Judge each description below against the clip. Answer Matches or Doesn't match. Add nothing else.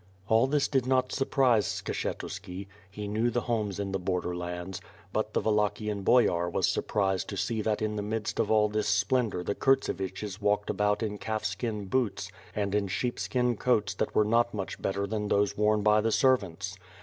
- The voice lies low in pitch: Matches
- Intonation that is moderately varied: Doesn't match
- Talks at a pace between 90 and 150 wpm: Doesn't match